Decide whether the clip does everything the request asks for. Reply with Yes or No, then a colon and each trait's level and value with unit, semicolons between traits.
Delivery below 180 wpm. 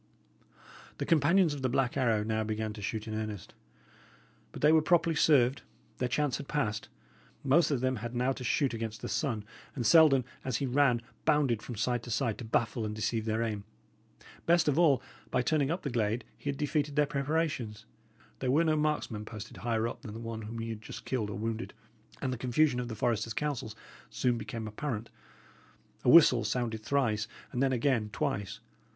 No: average, 195 wpm